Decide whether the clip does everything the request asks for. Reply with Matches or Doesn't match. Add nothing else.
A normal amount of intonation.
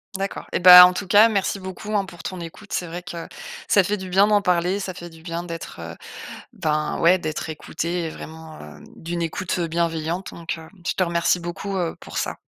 Doesn't match